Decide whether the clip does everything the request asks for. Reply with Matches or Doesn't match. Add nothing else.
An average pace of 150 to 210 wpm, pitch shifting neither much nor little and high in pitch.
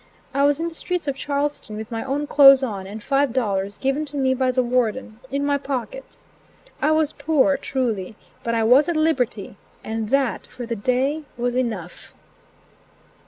Matches